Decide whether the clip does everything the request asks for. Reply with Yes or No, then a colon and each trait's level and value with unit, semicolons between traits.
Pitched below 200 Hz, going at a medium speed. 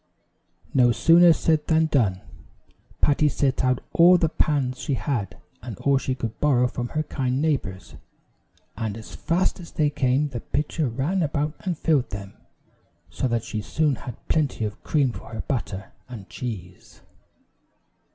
Yes: low, 135 Hz; average, 160 wpm